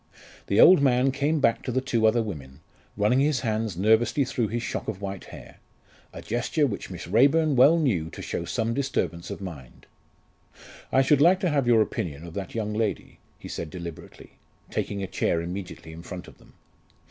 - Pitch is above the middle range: No, low, 110 Hz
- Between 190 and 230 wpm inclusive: Yes, average, 195 wpm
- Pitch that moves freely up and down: Yes, wide, 6.6 semitones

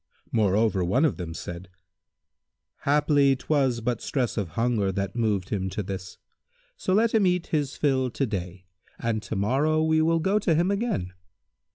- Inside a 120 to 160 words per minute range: No, average, 170 wpm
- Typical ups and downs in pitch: No, wide, 8.1 semitones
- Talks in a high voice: No, low, 125 Hz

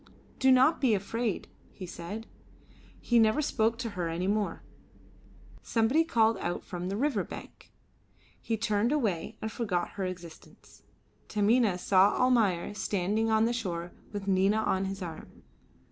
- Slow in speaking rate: No, average, 145 wpm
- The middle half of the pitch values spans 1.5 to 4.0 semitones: Yes, average, 3.7 semitones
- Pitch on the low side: No, high, 210 Hz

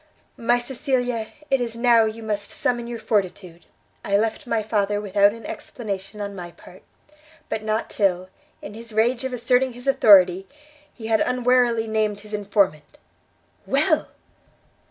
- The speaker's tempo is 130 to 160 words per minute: Yes, average, 150 wpm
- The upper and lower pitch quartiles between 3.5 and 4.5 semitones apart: No, average, 2.9 semitones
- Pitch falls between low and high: No, high, 220 Hz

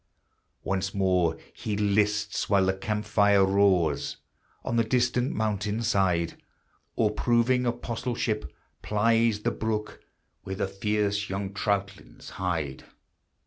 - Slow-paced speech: Yes, slow, 115 wpm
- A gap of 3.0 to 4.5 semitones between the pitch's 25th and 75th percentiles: No, narrow, 2.4 semitones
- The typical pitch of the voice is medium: No, low, 105 Hz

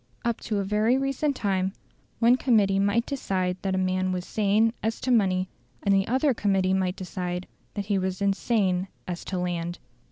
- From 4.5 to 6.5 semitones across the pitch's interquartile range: No, average, 3.2 semitones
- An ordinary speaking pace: Yes, average, 185 wpm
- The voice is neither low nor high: No, high, 195 Hz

